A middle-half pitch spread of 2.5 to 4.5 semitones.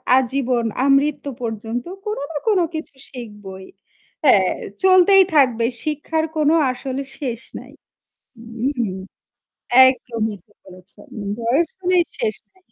No: average, 5.1 semitones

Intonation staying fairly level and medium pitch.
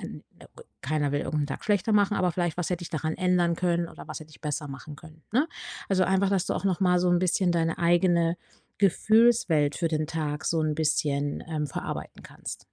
No: average, 3.1 semitones; medium, 170 Hz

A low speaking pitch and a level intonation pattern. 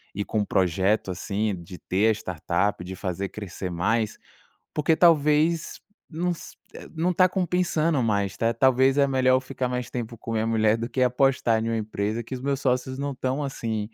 No: low, 115 Hz; average, 4.9 semitones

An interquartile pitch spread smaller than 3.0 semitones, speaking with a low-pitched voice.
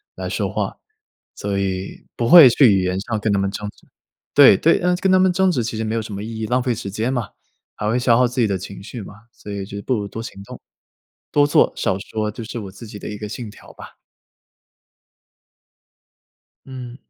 No: average, 3.6 semitones; low, 110 Hz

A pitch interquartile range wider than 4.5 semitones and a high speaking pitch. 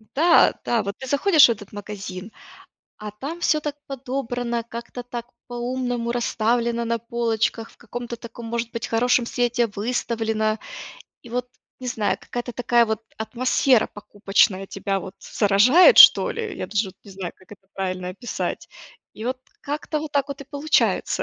No: average, 2.9 semitones; high, 235 Hz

